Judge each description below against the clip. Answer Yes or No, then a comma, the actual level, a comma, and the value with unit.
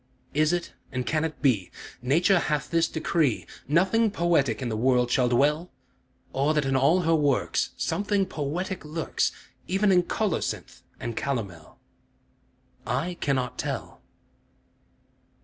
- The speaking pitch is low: No, medium, 150 Hz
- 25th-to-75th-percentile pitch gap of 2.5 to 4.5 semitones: No, average, 5.0 semitones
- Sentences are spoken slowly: Yes, slow, 130 wpm